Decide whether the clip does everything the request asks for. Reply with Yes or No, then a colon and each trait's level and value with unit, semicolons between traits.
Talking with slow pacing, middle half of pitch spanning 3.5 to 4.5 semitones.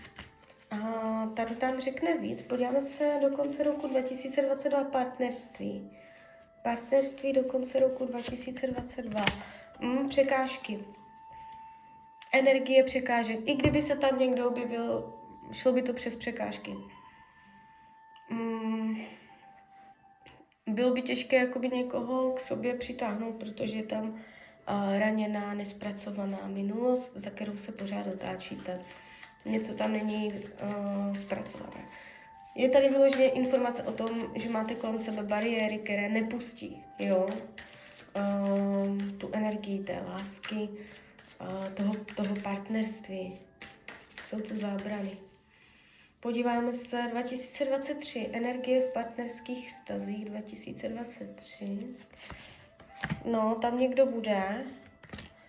Yes: slow, 105 wpm; average, 4.1 semitones